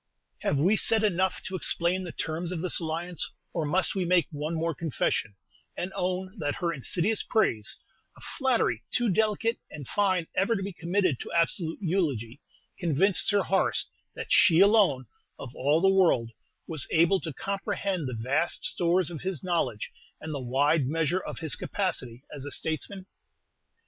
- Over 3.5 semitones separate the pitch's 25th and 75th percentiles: Yes, average, 4.1 semitones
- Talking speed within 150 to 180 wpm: Yes, average, 170 wpm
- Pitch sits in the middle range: Yes, medium, 170 Hz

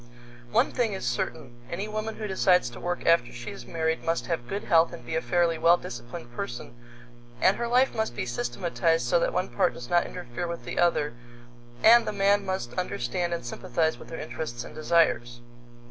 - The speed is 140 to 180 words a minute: No, average, 200 wpm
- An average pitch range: No, wide, 7.6 semitones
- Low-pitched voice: No, medium, 170 Hz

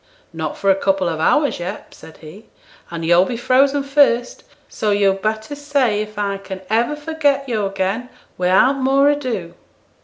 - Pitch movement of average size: No, wide, 6.3 semitones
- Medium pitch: No, high, 215 Hz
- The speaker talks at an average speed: Yes, average, 165 wpm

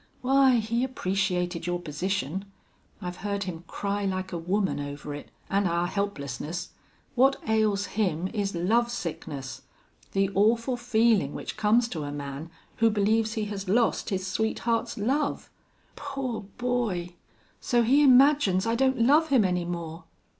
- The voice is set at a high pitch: Yes, high, 200 Hz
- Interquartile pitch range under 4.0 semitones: No, average, 4.9 semitones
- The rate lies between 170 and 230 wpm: No, average, 145 wpm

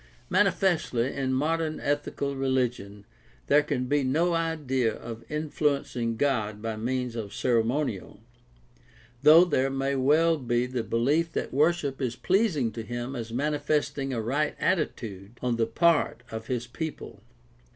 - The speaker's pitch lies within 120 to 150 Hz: Yes, low, 135 Hz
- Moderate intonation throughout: Yes, average, 4.3 semitones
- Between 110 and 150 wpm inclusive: Yes, average, 140 wpm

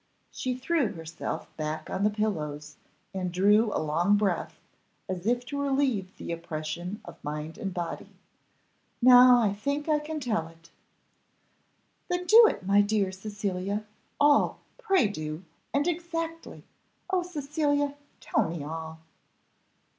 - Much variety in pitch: Yes, wide, 8.9 semitones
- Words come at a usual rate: No, slow, 130 wpm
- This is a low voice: No, high, 205 Hz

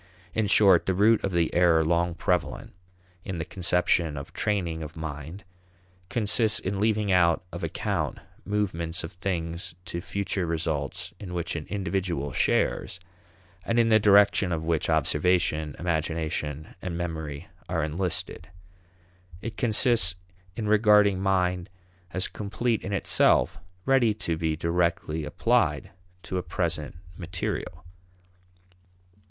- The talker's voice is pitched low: Yes, very low, 90 Hz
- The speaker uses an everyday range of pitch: Yes, average, 3.5 semitones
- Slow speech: Yes, slow, 130 wpm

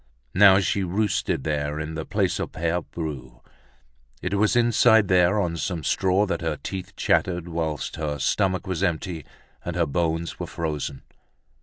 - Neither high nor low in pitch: No, very low, 85 Hz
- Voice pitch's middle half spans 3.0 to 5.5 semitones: Yes, average, 3.5 semitones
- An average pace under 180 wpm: Yes, average, 160 wpm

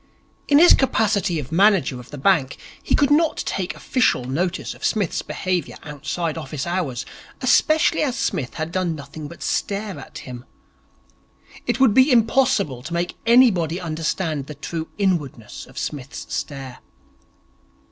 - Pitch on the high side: No, medium, 170 Hz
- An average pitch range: No, wide, 6.6 semitones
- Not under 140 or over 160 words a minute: Yes, average, 145 wpm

